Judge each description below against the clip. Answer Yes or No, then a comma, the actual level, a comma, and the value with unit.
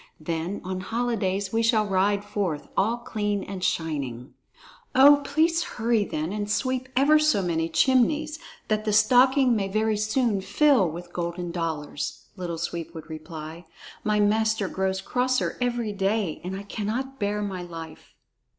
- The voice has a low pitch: No, high, 205 Hz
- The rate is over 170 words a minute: No, average, 155 wpm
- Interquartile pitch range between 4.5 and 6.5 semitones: Yes, average, 5.3 semitones